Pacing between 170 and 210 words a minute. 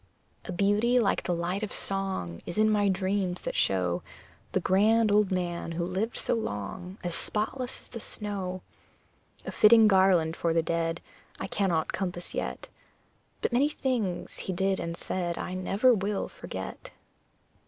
No: average, 160 wpm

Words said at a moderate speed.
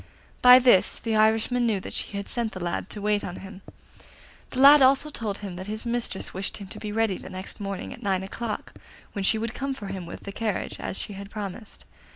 No: fast, 225 wpm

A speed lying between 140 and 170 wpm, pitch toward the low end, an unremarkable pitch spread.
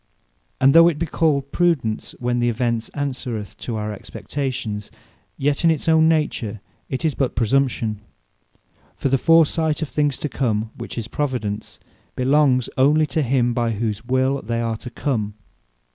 Yes: average, 160 wpm; low, 130 Hz; average, 4.2 semitones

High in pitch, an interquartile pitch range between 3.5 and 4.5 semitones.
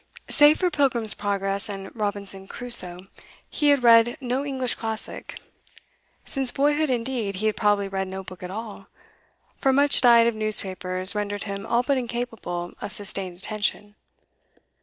Yes: high, 215 Hz; average, 4.0 semitones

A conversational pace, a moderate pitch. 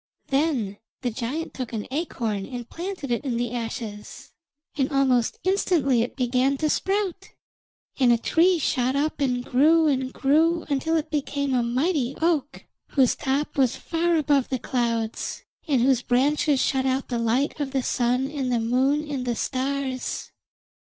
No: average, 165 wpm; very high, 265 Hz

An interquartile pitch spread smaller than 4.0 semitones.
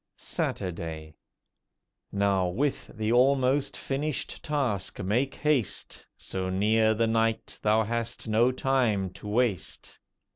No: average, 4.4 semitones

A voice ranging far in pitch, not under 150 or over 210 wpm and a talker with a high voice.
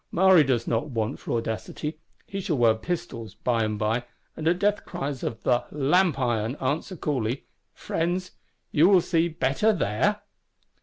No: wide, 7.1 semitones; average, 170 wpm; medium, 140 Hz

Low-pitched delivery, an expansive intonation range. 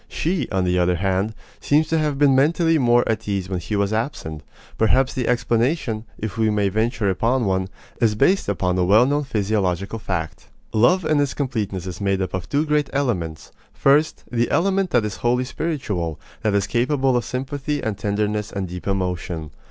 Yes: low, 110 Hz; wide, 5.9 semitones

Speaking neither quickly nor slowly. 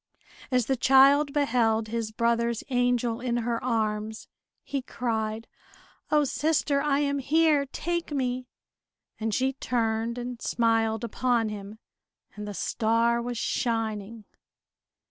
No: slow, 125 wpm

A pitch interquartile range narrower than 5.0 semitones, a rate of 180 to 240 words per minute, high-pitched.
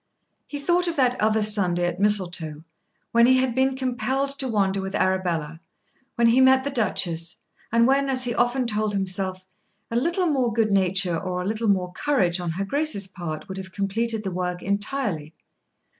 No: wide, 5.6 semitones; average, 185 wpm; high, 210 Hz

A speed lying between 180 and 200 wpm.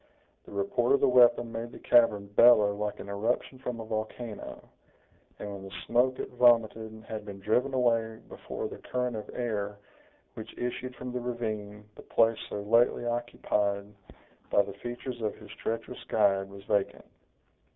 No: average, 165 wpm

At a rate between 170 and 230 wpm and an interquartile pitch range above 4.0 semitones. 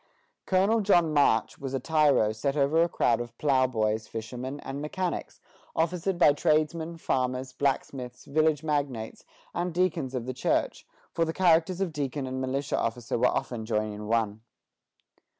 No: average, 155 wpm; average, 4.7 semitones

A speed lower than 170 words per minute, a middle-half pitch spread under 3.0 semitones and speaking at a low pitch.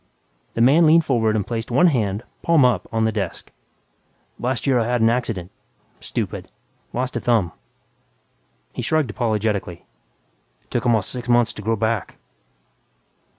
Yes: average, 150 wpm; narrow, 2.4 semitones; low, 115 Hz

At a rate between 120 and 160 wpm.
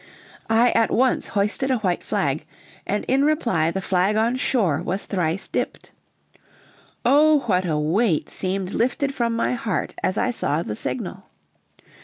Yes: average, 155 wpm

